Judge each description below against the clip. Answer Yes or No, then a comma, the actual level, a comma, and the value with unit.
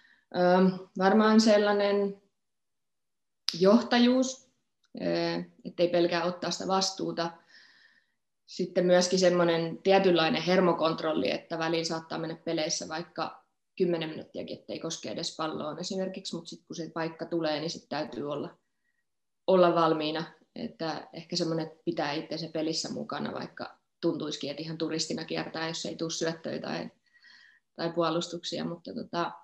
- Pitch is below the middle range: No, medium, 170 Hz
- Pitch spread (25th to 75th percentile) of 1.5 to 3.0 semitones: Yes, narrow, 2.6 semitones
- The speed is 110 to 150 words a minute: Yes, average, 120 wpm